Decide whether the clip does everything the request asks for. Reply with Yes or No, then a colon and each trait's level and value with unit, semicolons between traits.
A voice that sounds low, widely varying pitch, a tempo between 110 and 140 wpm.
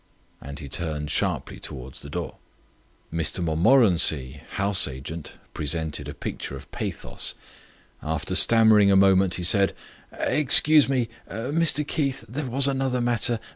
Yes: very low, 95 Hz; wide, 8.3 semitones; slow, 135 wpm